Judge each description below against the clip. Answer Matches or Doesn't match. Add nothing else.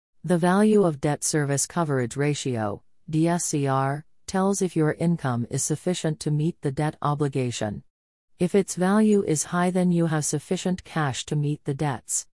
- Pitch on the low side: Doesn't match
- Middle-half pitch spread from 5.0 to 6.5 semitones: Doesn't match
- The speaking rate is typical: Matches